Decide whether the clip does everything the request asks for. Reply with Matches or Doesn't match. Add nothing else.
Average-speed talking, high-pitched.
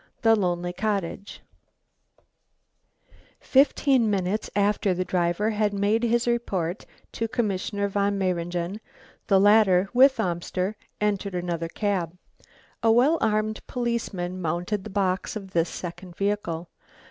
Doesn't match